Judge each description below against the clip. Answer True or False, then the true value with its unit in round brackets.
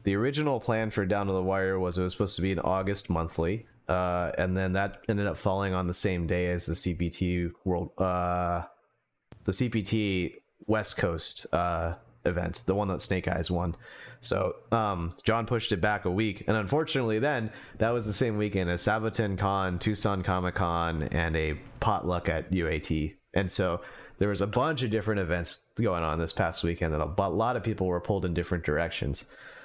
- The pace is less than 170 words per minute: False (195 wpm)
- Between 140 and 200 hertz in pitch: False (95 Hz)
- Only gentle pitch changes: False (3.5 semitones)